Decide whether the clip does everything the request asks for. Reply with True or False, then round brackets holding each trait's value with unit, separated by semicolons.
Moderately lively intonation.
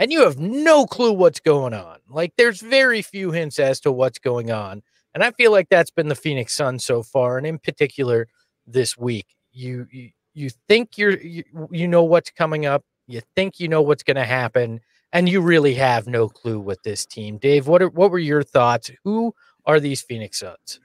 False (5.9 semitones)